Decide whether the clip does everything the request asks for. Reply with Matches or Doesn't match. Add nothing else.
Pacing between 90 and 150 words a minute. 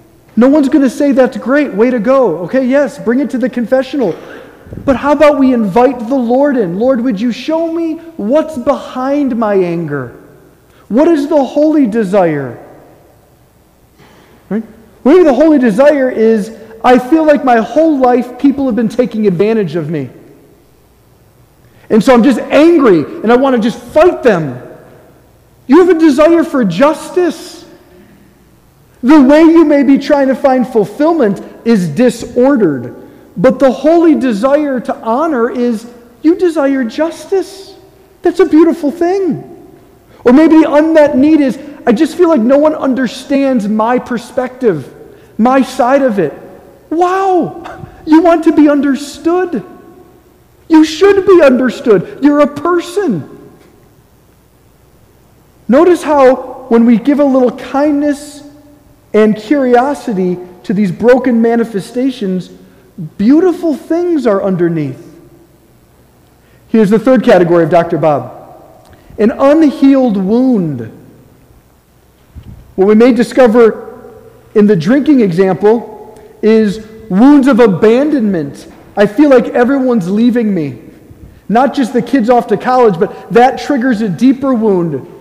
Matches